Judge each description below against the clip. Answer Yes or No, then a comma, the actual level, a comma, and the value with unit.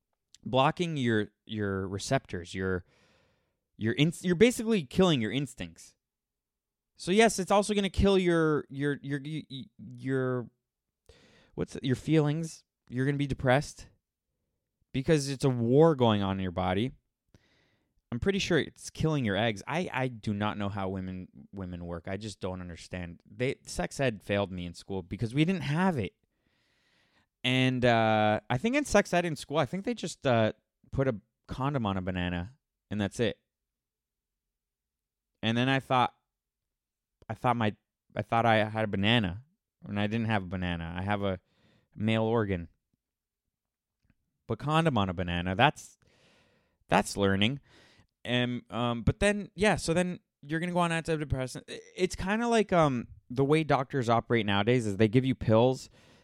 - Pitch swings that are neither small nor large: No, wide, 6.6 semitones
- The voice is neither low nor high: No, low, 120 Hz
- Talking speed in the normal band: Yes, average, 165 wpm